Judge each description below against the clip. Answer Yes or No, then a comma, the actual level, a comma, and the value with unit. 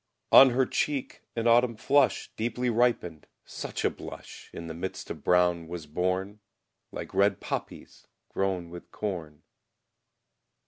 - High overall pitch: No, very low, 95 Hz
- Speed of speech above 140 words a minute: No, slow, 135 wpm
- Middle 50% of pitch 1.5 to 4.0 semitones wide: No, wide, 5.4 semitones